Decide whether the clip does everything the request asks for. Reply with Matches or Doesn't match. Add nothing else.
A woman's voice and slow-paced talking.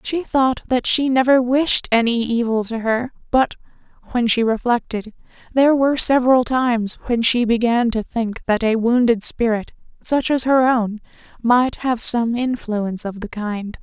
Doesn't match